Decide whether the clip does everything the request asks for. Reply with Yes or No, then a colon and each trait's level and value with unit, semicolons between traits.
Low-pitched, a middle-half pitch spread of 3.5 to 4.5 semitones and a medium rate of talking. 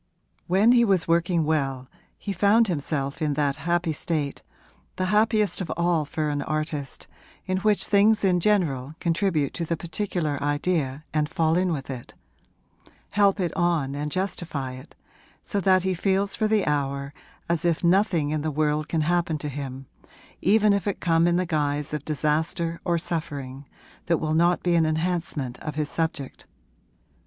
No: medium, 165 Hz; average, 3.8 semitones; average, 170 wpm